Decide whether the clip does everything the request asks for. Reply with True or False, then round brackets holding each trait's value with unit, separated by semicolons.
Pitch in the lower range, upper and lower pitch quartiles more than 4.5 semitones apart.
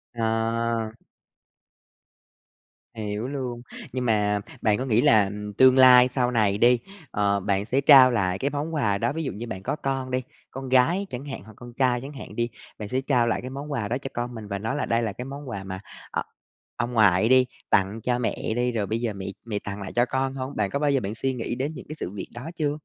False (120 Hz; 3.8 semitones)